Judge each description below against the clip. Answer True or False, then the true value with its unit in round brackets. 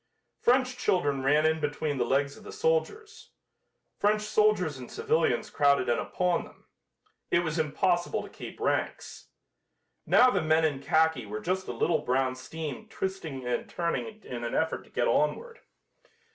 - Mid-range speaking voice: True (160 Hz)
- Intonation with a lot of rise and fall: True (7.0 semitones)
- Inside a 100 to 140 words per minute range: False (160 wpm)